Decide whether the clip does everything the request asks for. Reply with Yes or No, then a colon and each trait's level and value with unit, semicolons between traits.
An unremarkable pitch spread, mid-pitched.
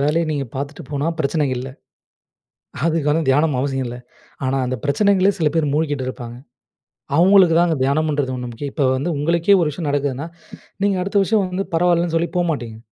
Yes: average, 3.7 semitones; medium, 150 Hz